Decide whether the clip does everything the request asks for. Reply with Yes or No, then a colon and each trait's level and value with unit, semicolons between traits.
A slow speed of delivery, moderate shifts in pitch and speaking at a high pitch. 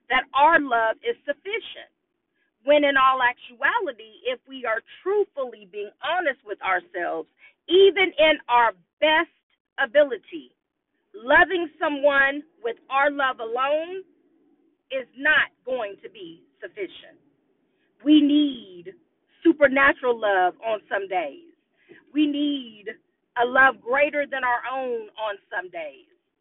Yes: slow, 120 wpm; average, 4.7 semitones; very high, 305 Hz